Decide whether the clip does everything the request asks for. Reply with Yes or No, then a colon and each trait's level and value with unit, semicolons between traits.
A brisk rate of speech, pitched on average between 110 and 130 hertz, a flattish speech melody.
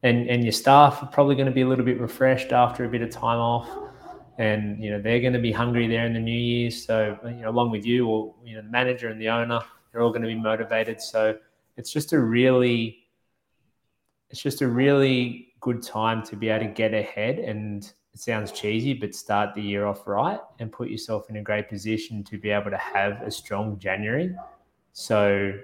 Yes: fast, 220 wpm; low, 115 Hz; narrow, 2.3 semitones